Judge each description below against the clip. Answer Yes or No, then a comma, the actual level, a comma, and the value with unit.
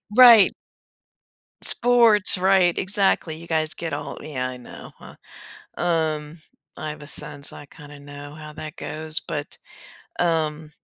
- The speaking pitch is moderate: Yes, medium, 155 Hz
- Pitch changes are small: No, average, 3.1 semitones